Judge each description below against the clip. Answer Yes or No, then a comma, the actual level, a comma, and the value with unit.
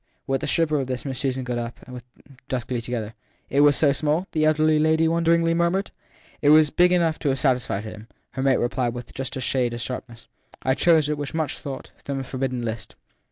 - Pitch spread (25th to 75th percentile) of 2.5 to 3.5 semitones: No, average, 3.9 semitones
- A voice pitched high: No, low, 135 Hz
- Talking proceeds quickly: Yes, fast, 240 wpm